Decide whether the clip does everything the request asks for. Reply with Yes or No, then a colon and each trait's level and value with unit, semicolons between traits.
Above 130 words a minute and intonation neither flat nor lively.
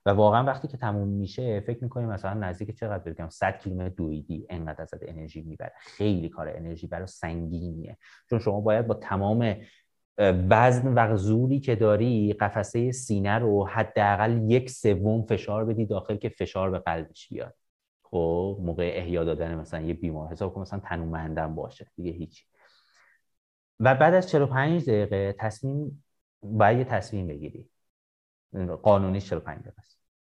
Yes: average, 145 wpm; average, 4.8 semitones